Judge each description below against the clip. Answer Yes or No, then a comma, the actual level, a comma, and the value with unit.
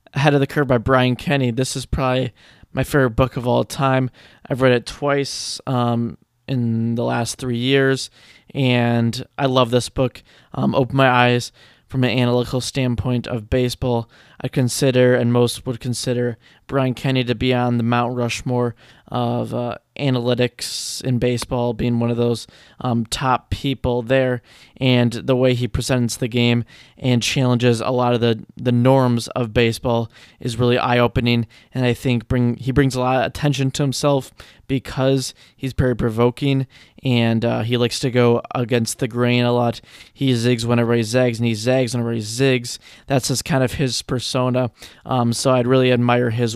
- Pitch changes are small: Yes, narrow, 1.6 semitones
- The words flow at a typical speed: Yes, average, 180 wpm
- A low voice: Yes, low, 125 Hz